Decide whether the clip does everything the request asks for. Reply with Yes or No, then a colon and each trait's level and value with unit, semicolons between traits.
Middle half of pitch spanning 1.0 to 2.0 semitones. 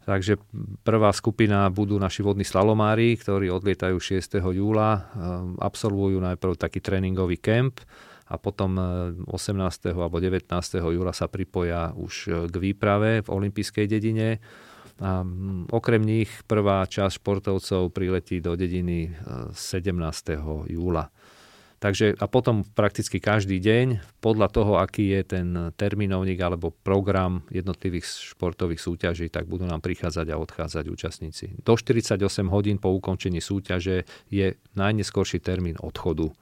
No: narrow, 2.6 semitones